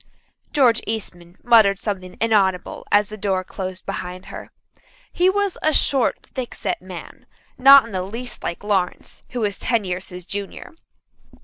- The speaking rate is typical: Yes, average, 150 wpm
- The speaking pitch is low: No, high, 205 Hz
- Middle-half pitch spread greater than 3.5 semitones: Yes, average, 4.3 semitones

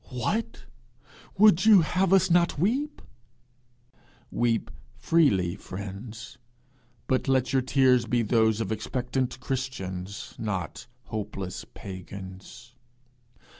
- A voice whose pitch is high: No, low, 120 Hz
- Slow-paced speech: Yes, slow, 95 wpm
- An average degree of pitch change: No, wide, 6.3 semitones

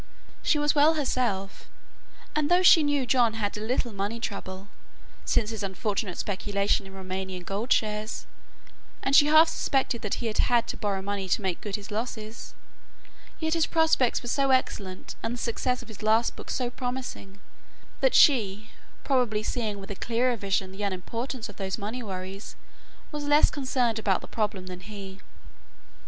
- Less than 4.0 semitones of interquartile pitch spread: No, average, 4.4 semitones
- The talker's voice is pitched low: No, high, 220 Hz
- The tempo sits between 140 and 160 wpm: No, average, 175 wpm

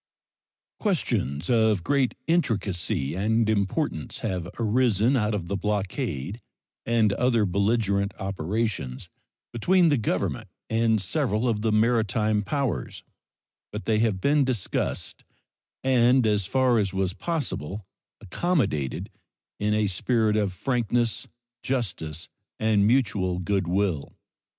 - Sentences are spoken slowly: Yes, slow, 115 wpm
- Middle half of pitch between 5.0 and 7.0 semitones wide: No, average, 3.7 semitones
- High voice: No, low, 110 Hz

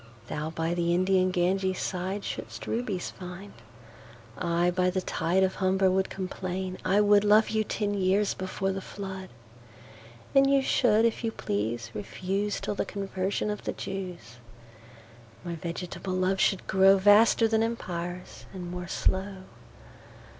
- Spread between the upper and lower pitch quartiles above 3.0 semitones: No, narrow, 2.6 semitones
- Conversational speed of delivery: No, slow, 125 wpm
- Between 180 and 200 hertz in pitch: Yes, medium, 185 Hz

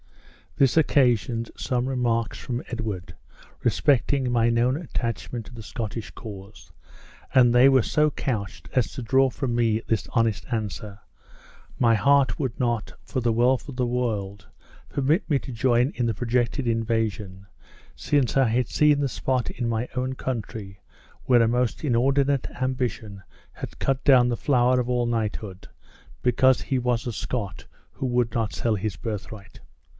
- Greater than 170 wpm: No, average, 160 wpm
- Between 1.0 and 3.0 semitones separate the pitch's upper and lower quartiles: Yes, narrow, 2.5 semitones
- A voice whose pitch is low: Yes, low, 120 Hz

